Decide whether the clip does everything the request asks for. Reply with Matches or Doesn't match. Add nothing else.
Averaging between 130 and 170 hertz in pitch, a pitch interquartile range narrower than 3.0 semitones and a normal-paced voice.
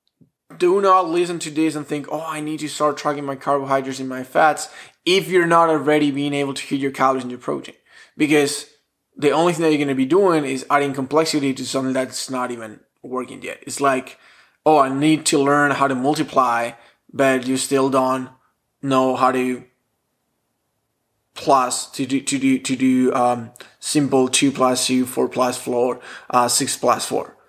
Matches